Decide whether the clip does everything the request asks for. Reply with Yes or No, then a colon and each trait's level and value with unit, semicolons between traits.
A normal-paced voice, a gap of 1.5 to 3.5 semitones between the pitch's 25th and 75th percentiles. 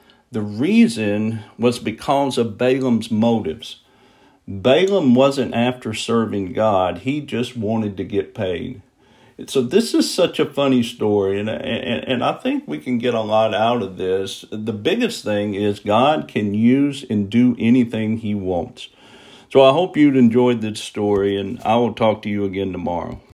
Yes: average, 160 wpm; average, 3.2 semitones